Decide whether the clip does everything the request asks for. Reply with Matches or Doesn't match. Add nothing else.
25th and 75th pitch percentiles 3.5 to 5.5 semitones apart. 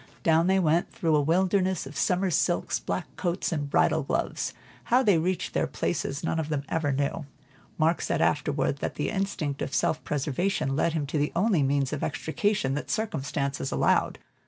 Matches